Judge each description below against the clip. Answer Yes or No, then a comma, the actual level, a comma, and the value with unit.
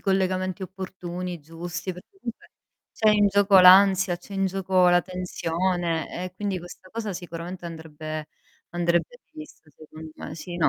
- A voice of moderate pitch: Yes, medium, 180 Hz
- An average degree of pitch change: No, narrow, 1.9 semitones